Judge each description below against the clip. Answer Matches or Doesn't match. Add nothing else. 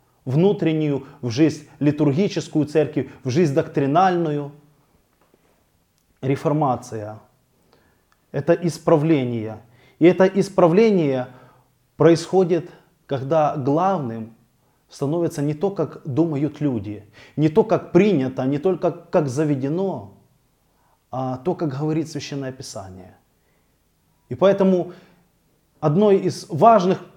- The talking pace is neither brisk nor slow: Doesn't match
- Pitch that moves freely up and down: Doesn't match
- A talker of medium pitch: Matches